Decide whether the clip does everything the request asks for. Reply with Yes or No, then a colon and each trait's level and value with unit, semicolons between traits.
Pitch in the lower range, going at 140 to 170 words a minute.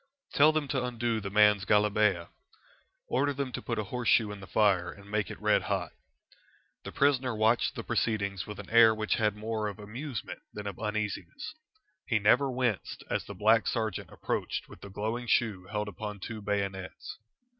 No: low, 110 Hz; average, 180 wpm